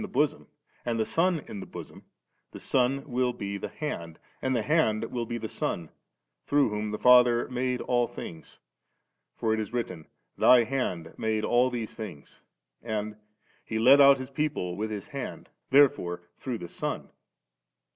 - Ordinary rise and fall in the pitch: Yes, average, 3.6 semitones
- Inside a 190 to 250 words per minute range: No, average, 175 wpm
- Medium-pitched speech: No, low, 120 Hz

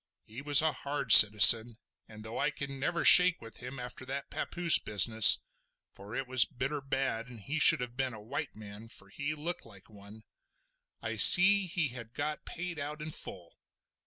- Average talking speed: Yes, average, 180 wpm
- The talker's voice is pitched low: Yes, low, 130 Hz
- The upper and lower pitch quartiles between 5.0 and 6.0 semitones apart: Yes, average, 5.3 semitones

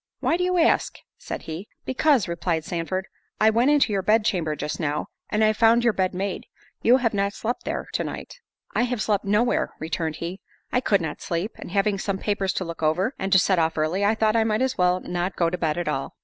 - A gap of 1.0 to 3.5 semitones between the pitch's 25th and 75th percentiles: No, average, 4.6 semitones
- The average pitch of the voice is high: Yes, high, 195 Hz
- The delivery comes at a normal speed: No, fast, 235 wpm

